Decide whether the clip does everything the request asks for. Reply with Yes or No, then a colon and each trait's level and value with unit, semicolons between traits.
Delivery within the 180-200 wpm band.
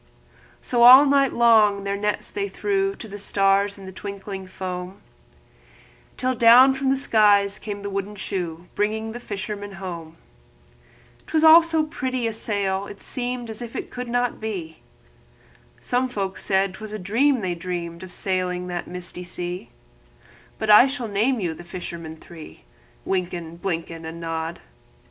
No: average, 165 wpm